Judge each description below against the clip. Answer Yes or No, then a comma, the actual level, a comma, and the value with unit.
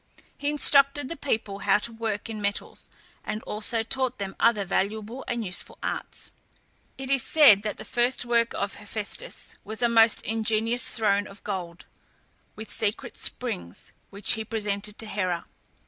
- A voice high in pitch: Yes, high, 220 Hz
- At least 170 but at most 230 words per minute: No, average, 160 wpm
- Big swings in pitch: No, average, 2.8 semitones